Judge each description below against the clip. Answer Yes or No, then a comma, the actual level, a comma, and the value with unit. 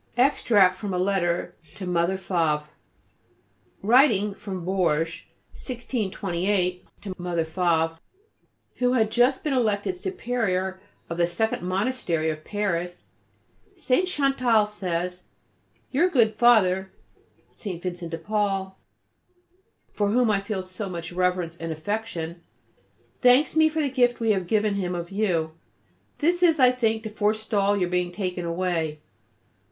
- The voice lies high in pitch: Yes, high, 195 Hz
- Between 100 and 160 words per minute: Yes, slow, 135 wpm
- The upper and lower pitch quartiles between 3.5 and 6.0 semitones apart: Yes, average, 4.4 semitones